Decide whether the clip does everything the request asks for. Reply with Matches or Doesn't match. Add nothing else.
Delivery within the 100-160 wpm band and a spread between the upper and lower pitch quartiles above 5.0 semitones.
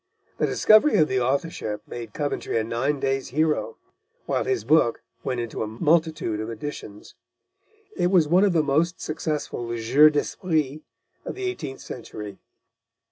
Matches